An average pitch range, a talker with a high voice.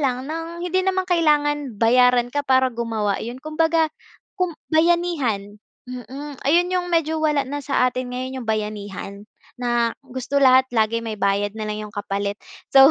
No: wide, 5.7 semitones; very high, 260 Hz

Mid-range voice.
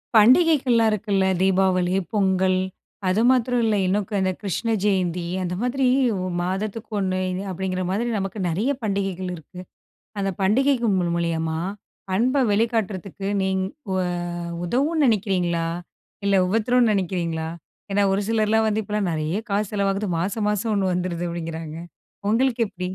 No: high, 195 Hz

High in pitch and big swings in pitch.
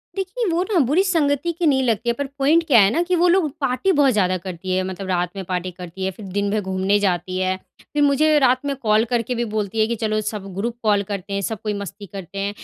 Yes: high, 215 Hz; wide, 6.8 semitones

